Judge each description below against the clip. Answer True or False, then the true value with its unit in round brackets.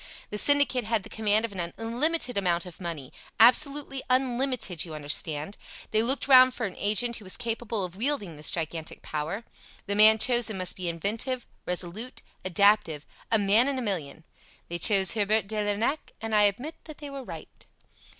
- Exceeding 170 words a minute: True (180 wpm)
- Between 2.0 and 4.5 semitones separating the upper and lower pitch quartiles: False (5.4 semitones)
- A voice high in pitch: True (215 Hz)